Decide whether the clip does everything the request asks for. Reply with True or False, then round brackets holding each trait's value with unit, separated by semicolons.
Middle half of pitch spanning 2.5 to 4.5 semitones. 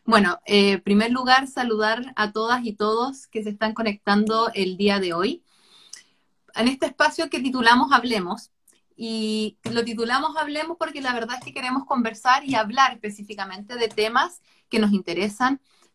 True (3.6 semitones)